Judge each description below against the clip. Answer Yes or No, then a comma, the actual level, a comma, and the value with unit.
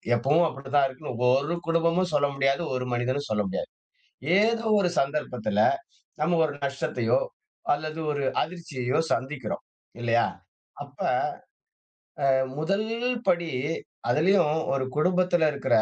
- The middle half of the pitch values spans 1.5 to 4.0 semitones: No, average, 4.6 semitones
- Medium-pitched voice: Yes, medium, 145 Hz